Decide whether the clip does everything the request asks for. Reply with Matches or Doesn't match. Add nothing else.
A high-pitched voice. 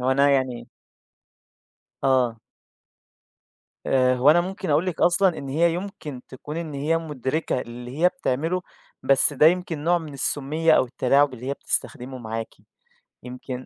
Doesn't match